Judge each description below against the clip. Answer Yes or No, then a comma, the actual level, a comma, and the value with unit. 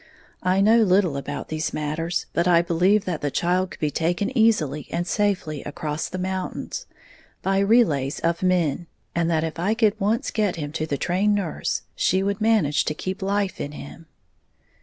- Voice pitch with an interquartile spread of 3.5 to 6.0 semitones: Yes, average, 4.2 semitones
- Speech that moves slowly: No, average, 180 wpm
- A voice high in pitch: No, medium, 180 Hz